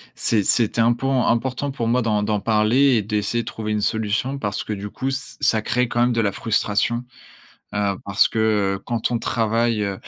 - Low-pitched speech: Yes, low, 110 Hz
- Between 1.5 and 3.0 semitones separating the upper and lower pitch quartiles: Yes, narrow, 2.4 semitones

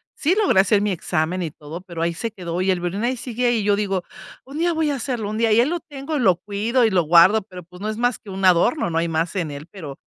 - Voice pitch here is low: No, high, 200 Hz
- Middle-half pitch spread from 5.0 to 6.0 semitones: Yes, wide, 5.5 semitones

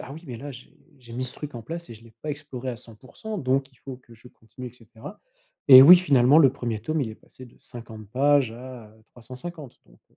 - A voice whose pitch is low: Yes, low, 125 Hz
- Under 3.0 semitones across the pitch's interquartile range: No, average, 3.4 semitones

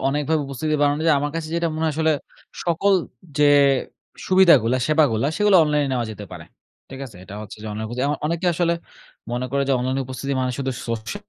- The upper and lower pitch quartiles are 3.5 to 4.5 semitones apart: Yes, average, 4.0 semitones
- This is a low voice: No, medium, 145 Hz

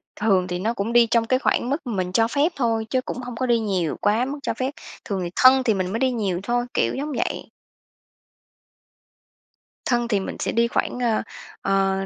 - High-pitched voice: Yes, high, 230 Hz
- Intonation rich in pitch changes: No, average, 4.3 semitones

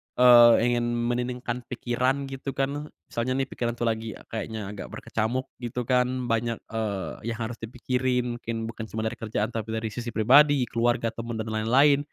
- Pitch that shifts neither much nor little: No, narrow, 2.0 semitones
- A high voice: No, low, 120 Hz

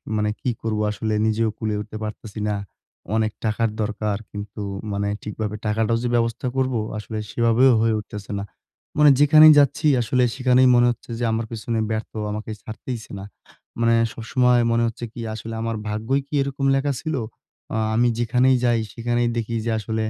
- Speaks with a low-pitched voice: Yes, low, 115 Hz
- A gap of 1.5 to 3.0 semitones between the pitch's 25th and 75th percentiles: Yes, narrow, 2.4 semitones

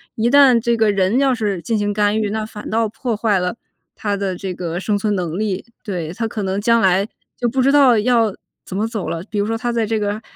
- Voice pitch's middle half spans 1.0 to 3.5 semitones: Yes, average, 2.8 semitones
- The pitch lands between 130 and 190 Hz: No, high, 210 Hz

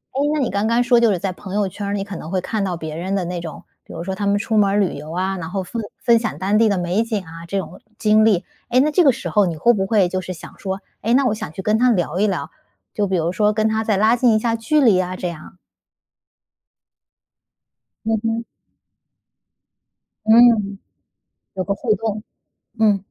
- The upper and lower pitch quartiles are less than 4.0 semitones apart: Yes, average, 3.3 semitones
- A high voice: Yes, high, 200 Hz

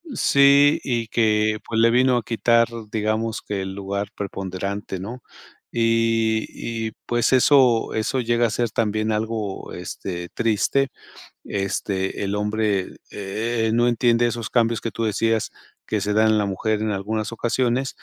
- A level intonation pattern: Yes, narrow, 2.2 semitones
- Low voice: Yes, low, 110 Hz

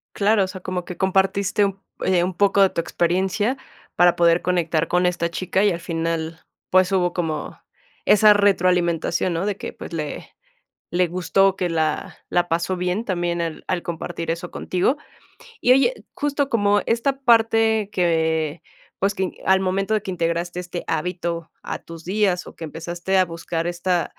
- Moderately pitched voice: Yes, medium, 180 Hz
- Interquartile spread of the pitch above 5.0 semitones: No, narrow, 2.6 semitones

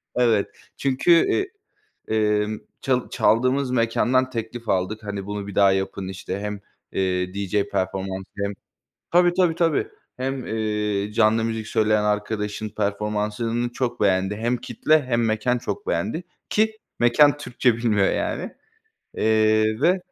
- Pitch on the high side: No, low, 110 Hz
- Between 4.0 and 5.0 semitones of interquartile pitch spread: No, average, 3.4 semitones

